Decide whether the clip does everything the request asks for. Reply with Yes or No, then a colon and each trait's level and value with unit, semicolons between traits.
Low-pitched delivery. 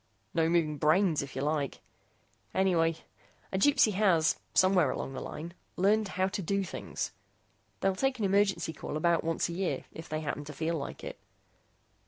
No: medium, 170 Hz